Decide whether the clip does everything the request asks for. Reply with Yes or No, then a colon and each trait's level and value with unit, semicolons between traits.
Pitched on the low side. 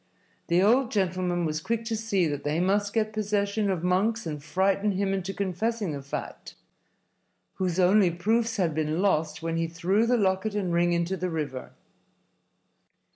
No: high, 190 Hz